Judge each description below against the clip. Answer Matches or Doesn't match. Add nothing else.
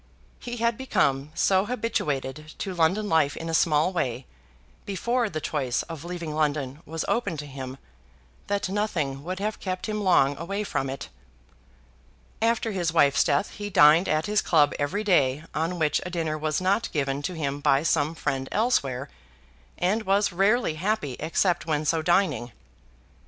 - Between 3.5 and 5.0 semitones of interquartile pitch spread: Doesn't match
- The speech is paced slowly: Doesn't match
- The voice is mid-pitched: Matches